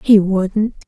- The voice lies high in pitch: Yes, high, 200 Hz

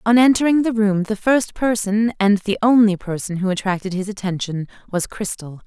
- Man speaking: No, female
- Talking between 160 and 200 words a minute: Yes, average, 180 wpm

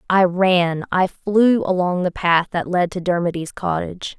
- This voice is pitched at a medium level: Yes, medium, 180 Hz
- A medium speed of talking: Yes, average, 170 wpm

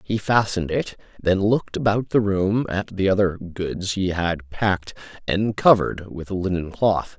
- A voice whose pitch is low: Yes, very low, 95 Hz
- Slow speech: No, average, 175 wpm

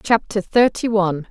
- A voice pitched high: Yes, high, 200 Hz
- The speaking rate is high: No, average, 140 wpm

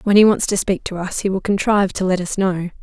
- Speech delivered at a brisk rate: Yes, fast, 300 wpm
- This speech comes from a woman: Yes, female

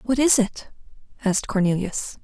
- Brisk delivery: No, slow, 135 wpm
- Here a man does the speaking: No, female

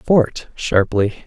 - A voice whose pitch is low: Yes, low, 120 Hz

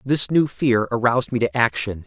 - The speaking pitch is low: Yes, low, 125 Hz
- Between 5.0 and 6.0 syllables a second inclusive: Yes, 5.2 syllables/s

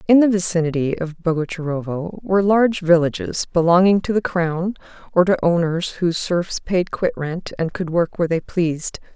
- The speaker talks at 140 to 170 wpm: Yes, average, 165 wpm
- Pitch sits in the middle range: Yes, medium, 175 Hz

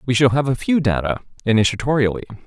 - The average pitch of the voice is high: No, low, 120 Hz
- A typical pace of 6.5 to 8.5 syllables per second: Yes, 7.0 syllables/s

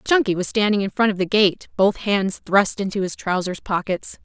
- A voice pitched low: No, high, 200 Hz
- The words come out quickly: Yes, fast, 210 wpm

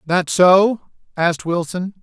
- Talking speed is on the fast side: No, slow, 120 wpm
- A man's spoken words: Yes, male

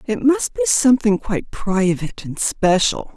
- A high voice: Yes, high, 225 Hz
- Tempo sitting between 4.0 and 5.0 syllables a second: Yes, 4.8 syllables/s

